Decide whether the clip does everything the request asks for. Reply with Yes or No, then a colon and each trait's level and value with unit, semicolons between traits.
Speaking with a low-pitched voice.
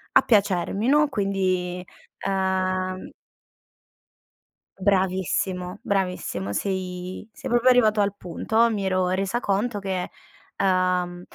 No: high, 190 Hz